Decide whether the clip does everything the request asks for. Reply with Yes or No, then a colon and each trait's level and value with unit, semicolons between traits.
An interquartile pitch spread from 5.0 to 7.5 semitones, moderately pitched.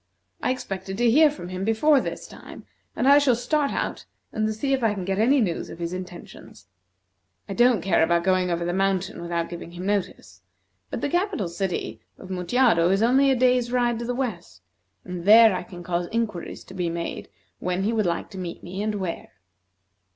No: wide, 5.4 semitones; high, 195 Hz